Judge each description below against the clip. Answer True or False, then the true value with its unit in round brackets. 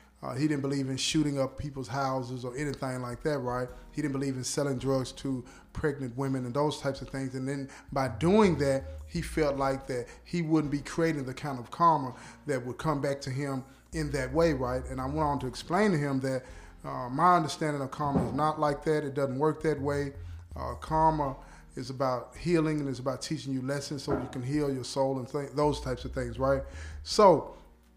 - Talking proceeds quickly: True (220 wpm)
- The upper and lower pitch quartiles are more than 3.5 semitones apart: False (2.4 semitones)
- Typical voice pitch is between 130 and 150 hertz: True (135 Hz)